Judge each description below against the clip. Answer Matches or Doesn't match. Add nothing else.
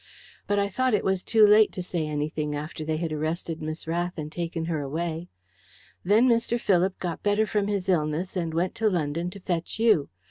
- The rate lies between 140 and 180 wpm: Doesn't match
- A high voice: Doesn't match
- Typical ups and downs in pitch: Matches